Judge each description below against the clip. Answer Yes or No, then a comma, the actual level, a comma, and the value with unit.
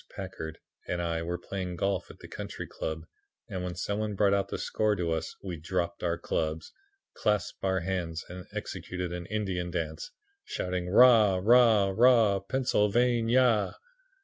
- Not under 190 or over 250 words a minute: No, average, 150 wpm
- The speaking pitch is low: Yes, very low, 95 Hz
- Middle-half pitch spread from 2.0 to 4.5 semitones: Yes, average, 3.4 semitones